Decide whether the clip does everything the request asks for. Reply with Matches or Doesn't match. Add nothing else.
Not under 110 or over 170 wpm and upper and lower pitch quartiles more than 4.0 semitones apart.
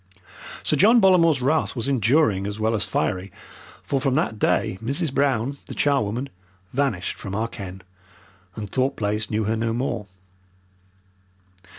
Matches